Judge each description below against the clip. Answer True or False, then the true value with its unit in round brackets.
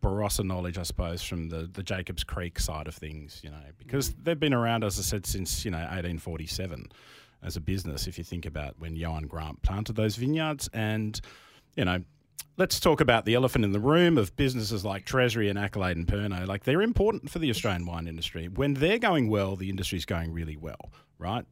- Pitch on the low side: True (95 Hz)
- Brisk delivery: True (210 wpm)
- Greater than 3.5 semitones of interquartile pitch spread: True (5.2 semitones)